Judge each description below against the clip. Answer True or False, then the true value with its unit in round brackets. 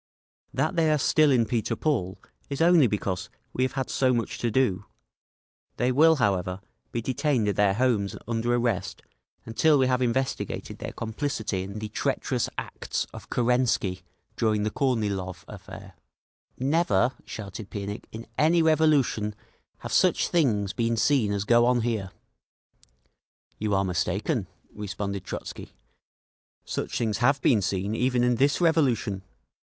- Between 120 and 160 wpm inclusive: True (145 wpm)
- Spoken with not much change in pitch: False (4.4 semitones)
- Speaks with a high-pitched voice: False (115 Hz)